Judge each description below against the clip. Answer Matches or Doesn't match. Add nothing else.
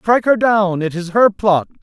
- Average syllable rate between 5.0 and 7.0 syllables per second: Doesn't match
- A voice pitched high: Matches